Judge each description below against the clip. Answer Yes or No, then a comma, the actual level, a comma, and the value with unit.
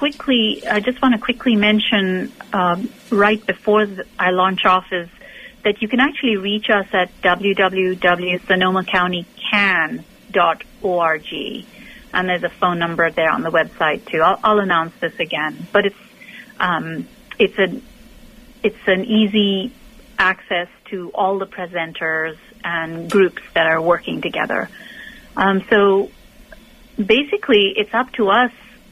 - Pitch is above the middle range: Yes, high, 200 Hz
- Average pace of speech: No, slow, 130 wpm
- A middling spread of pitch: Yes, average, 4.1 semitones